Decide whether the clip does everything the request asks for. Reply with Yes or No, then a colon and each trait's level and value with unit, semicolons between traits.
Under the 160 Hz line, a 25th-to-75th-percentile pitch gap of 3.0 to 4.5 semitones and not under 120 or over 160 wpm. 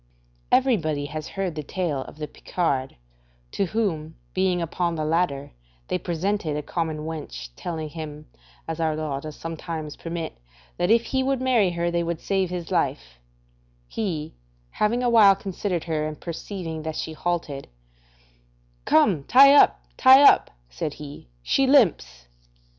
No: medium, 165 Hz; average, 4.1 semitones; average, 155 wpm